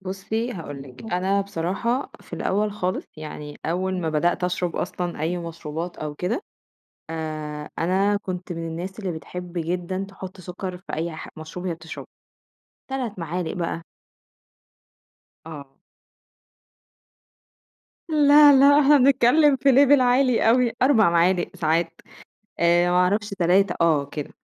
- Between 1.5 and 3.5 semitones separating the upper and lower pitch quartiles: No, average, 4.0 semitones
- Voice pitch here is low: No, medium, 180 Hz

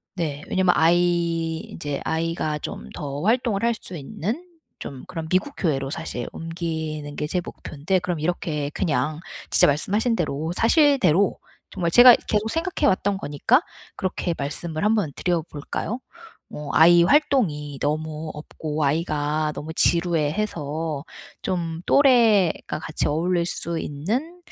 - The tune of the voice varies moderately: Yes, average, 4.1 semitones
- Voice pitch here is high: No, medium, 165 Hz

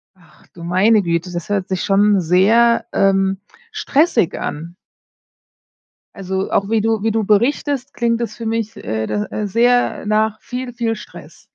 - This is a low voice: No, high, 210 Hz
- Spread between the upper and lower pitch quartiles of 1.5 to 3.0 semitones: No, average, 3.5 semitones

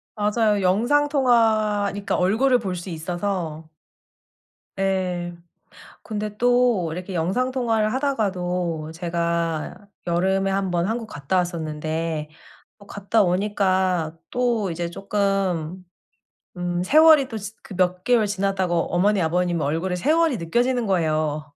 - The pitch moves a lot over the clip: No, average, 3.9 semitones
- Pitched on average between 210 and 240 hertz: No, high, 190 Hz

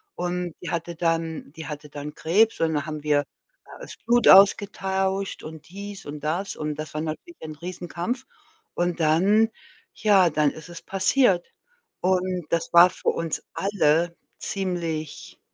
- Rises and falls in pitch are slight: No, average, 3.6 semitones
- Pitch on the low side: No, medium, 170 Hz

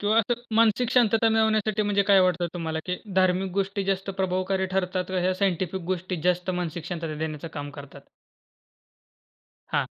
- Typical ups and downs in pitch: No, narrow, 2.3 semitones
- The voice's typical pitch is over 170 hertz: Yes, medium, 185 Hz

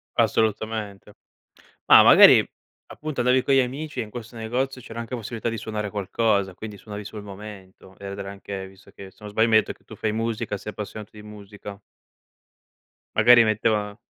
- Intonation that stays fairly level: Yes, narrow, 2.2 semitones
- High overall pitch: No, low, 110 Hz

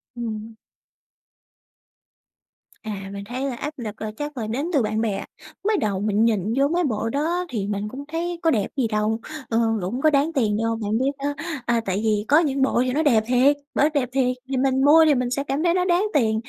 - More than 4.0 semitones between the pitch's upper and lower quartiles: Yes, average, 4.9 semitones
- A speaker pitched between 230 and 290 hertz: Yes, very high, 250 Hz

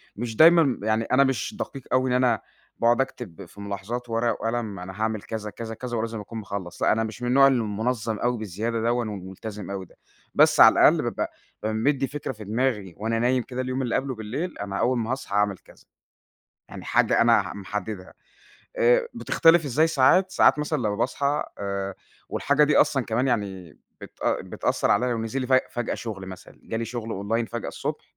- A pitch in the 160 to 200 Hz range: No, low, 115 Hz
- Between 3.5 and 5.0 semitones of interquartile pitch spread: Yes, average, 3.8 semitones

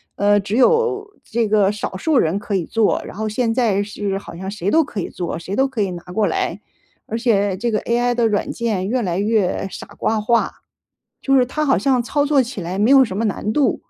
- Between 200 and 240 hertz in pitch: Yes, high, 220 Hz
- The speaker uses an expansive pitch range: No, average, 3.9 semitones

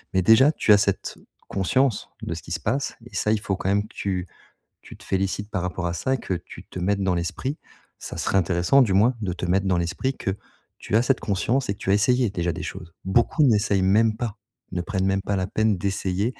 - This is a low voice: Yes, low, 100 Hz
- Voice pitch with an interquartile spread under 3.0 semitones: No, average, 3.4 semitones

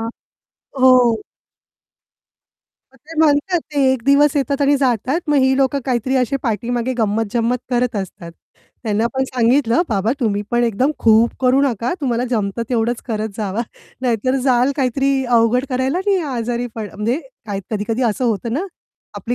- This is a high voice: Yes, high, 245 Hz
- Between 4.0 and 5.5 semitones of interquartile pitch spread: No, average, 2.8 semitones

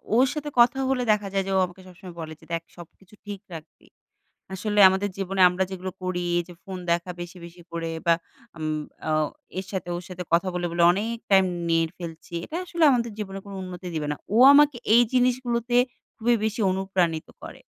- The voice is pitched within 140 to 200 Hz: Yes, high, 190 Hz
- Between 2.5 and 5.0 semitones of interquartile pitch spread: Yes, average, 4.1 semitones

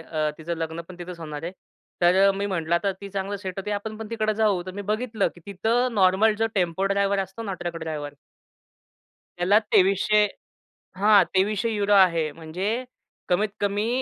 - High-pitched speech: Yes, high, 195 Hz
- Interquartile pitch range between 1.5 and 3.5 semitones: Yes, average, 3.1 semitones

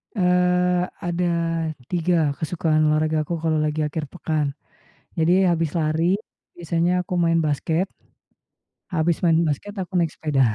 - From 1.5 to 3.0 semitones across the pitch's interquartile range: Yes, narrow, 2.5 semitones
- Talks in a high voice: No, medium, 165 Hz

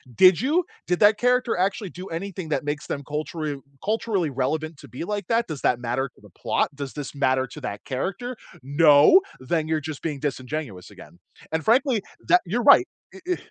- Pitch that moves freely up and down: Yes, wide, 6.2 semitones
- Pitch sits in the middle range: Yes, medium, 155 Hz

